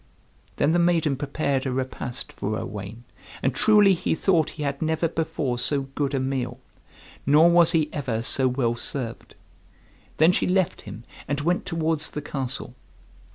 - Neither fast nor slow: Yes, average, 160 wpm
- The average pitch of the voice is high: No, medium, 145 Hz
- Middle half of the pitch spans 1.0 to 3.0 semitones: No, average, 3.9 semitones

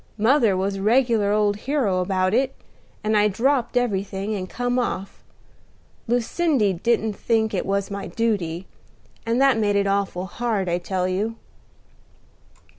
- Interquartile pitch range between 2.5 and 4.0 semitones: Yes, average, 3.6 semitones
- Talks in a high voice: Yes, high, 210 Hz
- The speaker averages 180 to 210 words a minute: No, average, 145 wpm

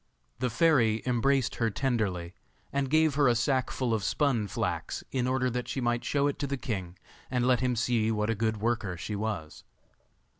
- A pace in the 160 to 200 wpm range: Yes, average, 195 wpm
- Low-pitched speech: Yes, low, 120 Hz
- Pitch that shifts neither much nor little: Yes, average, 3.3 semitones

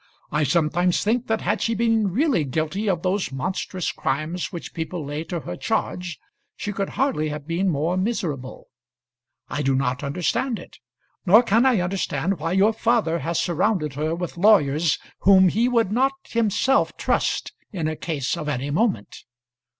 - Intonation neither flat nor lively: No, wide, 5.7 semitones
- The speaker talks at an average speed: Yes, average, 165 wpm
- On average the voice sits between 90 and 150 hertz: No, medium, 180 Hz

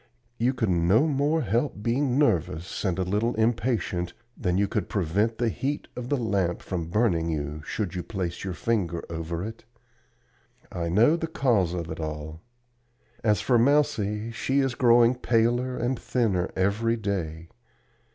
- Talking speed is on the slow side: No, average, 160 wpm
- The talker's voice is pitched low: Yes, low, 105 Hz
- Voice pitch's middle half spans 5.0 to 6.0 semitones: Yes, wide, 5.6 semitones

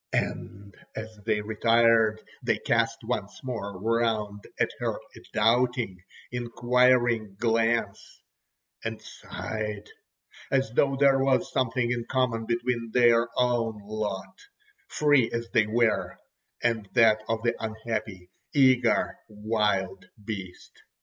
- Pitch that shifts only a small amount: Yes, narrow, 2.1 semitones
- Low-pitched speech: Yes, low, 115 Hz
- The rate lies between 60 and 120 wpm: Yes, slow, 110 wpm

